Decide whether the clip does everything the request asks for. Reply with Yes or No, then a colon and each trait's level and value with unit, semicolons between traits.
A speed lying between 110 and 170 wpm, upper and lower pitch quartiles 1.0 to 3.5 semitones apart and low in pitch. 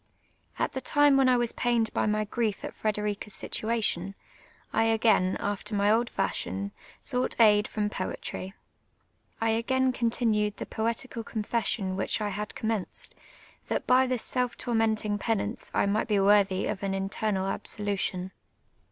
No: average, 150 wpm; narrow, 2.5 semitones; high, 215 Hz